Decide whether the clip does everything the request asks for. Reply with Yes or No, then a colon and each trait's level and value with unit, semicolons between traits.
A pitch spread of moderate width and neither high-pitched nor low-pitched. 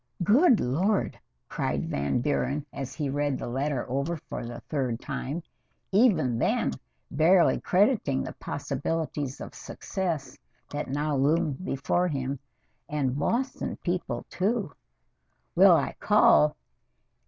Yes: average, 4.9 semitones; medium, 145 Hz